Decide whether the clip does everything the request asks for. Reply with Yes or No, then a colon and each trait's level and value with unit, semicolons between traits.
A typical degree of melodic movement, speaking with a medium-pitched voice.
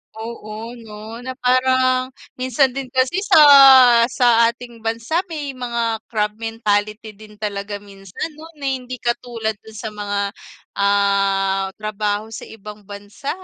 No: average, 3.3 semitones; high, 225 Hz